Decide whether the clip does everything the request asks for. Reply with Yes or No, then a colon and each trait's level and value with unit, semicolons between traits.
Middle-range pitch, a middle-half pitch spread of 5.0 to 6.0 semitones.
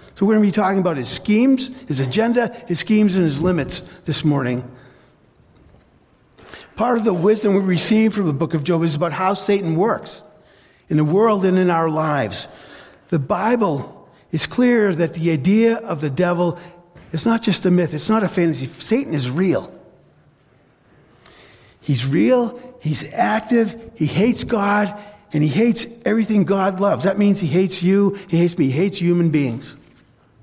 Yes: medium, 180 Hz; wide, 5.5 semitones